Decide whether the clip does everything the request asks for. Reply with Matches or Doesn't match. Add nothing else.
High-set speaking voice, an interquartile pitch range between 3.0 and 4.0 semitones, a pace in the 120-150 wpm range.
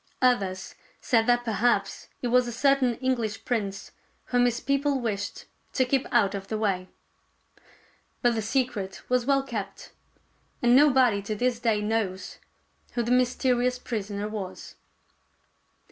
Matches